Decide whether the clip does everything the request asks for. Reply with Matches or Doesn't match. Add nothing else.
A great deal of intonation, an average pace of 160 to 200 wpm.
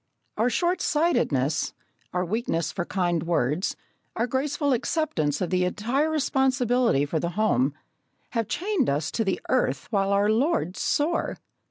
Doesn't match